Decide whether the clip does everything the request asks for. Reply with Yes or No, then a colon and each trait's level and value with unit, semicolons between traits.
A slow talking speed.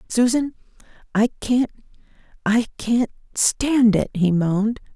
Yes: slow, 95 wpm